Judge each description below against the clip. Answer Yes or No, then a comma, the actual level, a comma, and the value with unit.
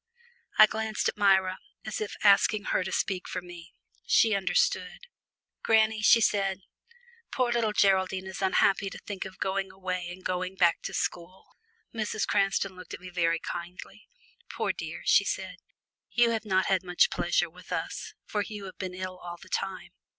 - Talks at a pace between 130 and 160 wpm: No, average, 175 wpm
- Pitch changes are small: Yes, narrow, 2.2 semitones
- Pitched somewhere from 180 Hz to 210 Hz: Yes, high, 190 Hz